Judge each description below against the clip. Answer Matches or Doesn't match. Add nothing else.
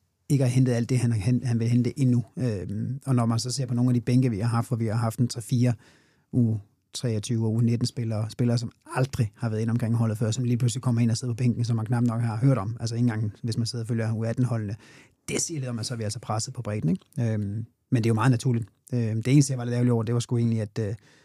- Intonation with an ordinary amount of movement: Doesn't match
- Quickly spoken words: Matches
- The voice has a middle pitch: Doesn't match